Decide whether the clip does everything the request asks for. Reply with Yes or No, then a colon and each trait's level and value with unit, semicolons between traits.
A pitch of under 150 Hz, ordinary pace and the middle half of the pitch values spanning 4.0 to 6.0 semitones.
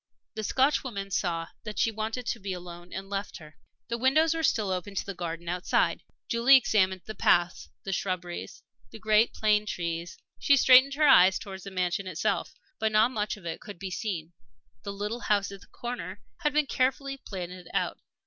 No: high, 200 Hz; average, 190 wpm; average, 4.5 semitones